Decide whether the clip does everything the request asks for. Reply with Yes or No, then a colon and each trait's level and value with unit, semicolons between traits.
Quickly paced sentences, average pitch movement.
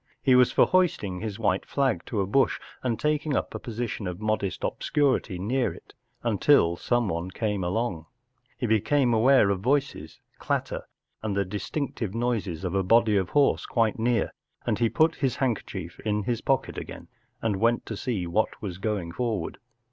No: average, 175 wpm; average, 4.4 semitones